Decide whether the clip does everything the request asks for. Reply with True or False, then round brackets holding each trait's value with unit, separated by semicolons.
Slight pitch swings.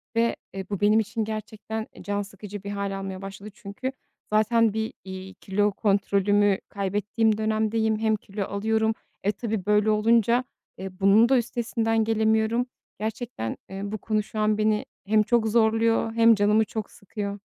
True (1.7 semitones)